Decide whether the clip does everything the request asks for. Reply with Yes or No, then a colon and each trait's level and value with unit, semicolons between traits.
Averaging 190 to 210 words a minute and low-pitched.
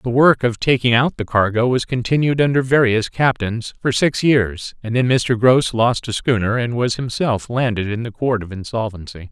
Yes: average, 200 wpm; low, 120 Hz